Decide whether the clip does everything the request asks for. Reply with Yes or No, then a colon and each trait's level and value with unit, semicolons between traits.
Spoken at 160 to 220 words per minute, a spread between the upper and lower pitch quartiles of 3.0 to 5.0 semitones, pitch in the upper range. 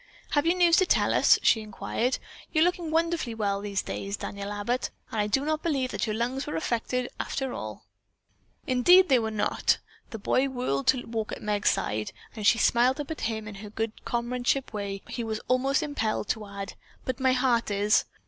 Yes: average, 200 wpm; average, 4.3 semitones; high, 235 Hz